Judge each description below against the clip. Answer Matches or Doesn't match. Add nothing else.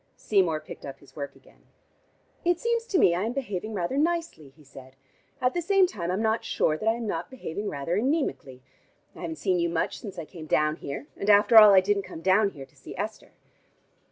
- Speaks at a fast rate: Matches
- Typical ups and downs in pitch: Doesn't match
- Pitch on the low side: Doesn't match